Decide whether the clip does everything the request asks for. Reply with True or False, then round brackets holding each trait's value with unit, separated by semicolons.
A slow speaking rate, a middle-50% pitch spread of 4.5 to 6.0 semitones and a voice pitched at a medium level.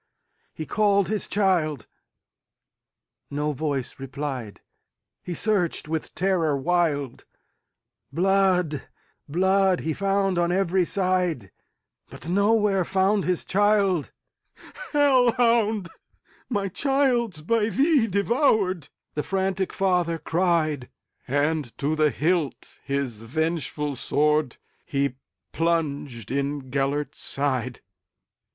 True (85 wpm; 5.1 semitones; 175 Hz)